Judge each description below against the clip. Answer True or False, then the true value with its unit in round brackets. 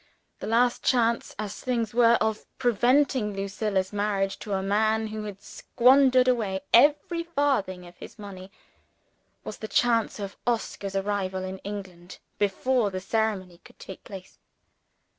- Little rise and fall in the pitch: False (3.6 semitones)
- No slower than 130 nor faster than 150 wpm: True (140 wpm)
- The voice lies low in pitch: False (210 Hz)